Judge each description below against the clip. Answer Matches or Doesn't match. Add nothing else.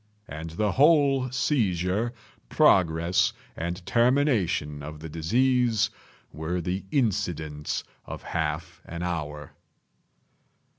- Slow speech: Matches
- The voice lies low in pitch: Matches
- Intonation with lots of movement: Matches